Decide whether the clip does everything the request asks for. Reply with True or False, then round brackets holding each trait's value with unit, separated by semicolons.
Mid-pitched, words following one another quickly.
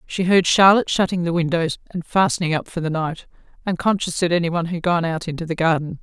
True (170 Hz; 220 wpm)